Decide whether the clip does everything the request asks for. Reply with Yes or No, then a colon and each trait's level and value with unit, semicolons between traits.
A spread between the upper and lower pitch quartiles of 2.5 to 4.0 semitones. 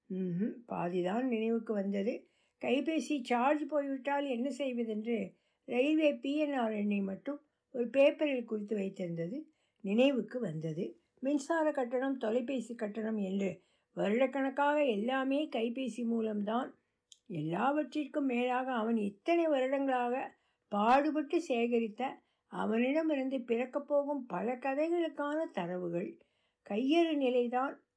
No: average, 4.5 semitones